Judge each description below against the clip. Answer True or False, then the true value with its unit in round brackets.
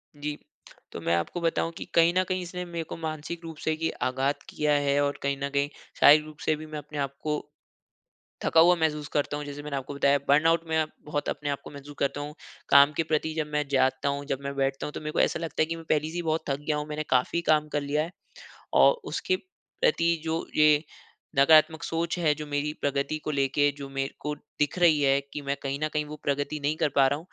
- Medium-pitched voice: True (150 Hz)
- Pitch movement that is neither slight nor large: False (2.0 semitones)